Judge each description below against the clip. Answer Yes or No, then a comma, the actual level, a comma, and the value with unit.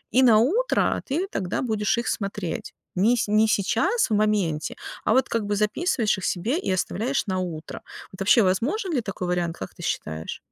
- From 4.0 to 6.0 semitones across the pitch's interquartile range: Yes, average, 4.6 semitones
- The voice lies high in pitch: Yes, high, 210 Hz